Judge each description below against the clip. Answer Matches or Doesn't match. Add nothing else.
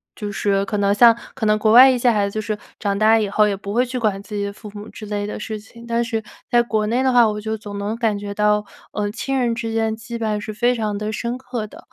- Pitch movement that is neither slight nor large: Doesn't match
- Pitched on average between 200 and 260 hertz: Matches